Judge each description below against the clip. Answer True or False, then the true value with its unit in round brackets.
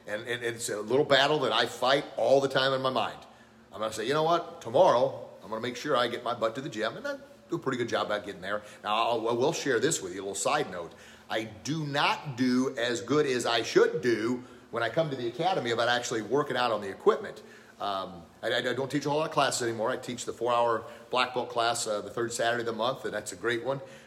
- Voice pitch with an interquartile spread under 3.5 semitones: False (4.0 semitones)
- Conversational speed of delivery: False (270 wpm)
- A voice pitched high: False (125 Hz)